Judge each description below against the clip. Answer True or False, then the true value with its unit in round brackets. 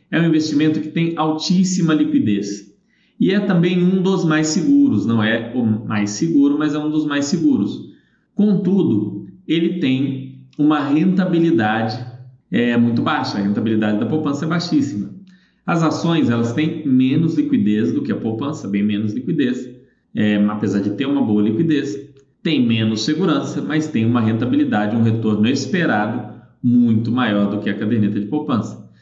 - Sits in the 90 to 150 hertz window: True (140 Hz)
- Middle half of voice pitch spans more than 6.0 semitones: True (6.6 semitones)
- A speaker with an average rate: True (160 wpm)